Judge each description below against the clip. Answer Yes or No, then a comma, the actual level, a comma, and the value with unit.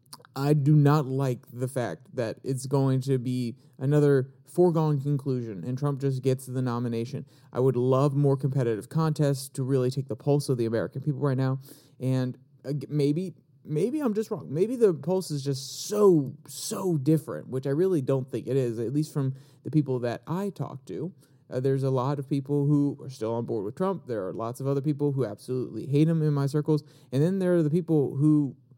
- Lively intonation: No, narrow, 2.5 semitones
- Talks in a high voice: No, medium, 140 Hz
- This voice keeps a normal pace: No, fast, 210 wpm